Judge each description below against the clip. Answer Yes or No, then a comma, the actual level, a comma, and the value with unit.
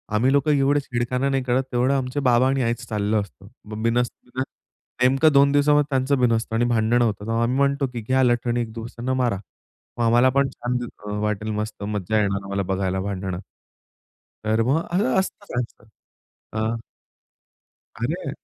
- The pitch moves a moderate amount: Yes, average, 3.6 semitones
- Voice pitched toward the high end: No, low, 120 Hz